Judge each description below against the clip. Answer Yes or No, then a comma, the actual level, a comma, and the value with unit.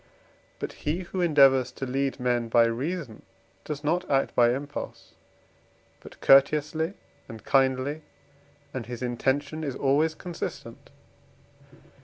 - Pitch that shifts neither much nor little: Yes, average, 3.4 semitones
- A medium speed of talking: No, slow, 120 wpm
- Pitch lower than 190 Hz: Yes, low, 135 Hz